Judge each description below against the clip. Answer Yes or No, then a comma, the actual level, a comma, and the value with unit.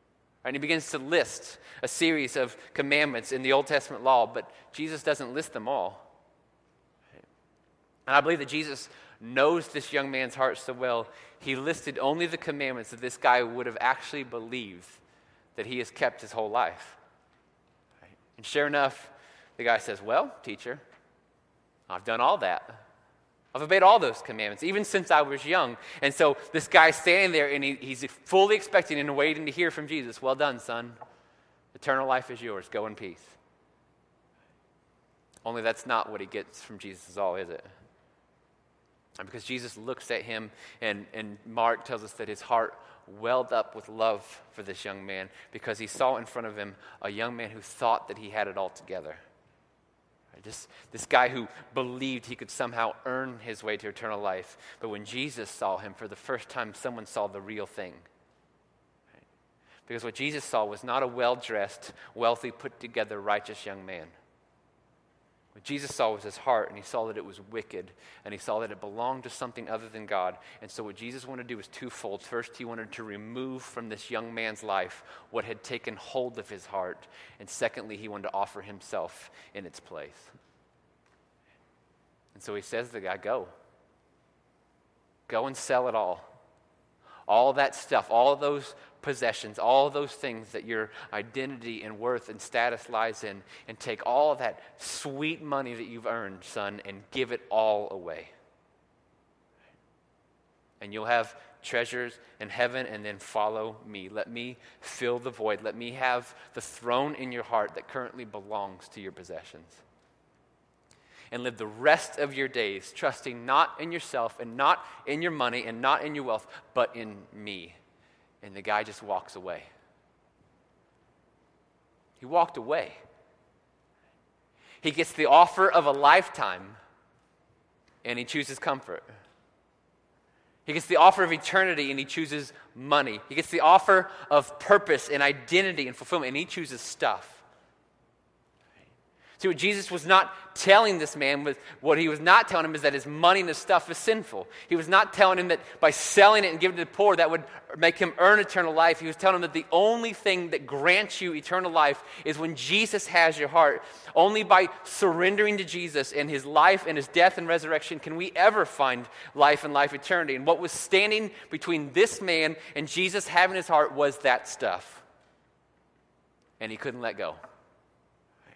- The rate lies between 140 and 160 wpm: No, average, 180 wpm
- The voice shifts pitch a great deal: Yes, wide, 5.9 semitones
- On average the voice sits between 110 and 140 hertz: Yes, low, 135 Hz